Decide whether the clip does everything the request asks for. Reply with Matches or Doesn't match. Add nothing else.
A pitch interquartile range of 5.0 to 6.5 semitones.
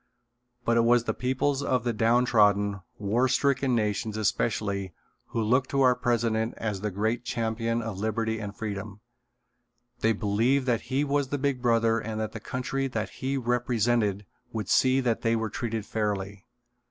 Doesn't match